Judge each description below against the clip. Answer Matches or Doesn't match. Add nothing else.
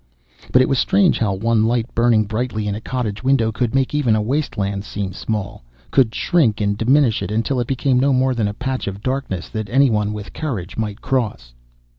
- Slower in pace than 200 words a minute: Doesn't match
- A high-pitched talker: Doesn't match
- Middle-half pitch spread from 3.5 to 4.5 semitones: Matches